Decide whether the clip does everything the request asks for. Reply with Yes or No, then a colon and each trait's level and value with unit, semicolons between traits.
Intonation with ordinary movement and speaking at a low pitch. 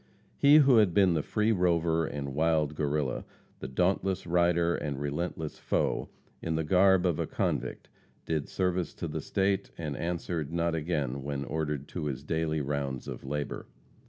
Yes: average, 3.4 semitones; very low, 80 Hz